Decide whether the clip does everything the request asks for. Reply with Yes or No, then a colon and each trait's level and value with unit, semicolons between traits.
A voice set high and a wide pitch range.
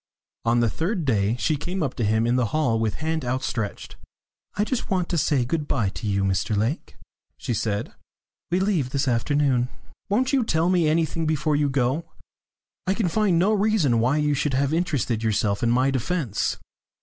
No: medium, 140 Hz; wide, 6.2 semitones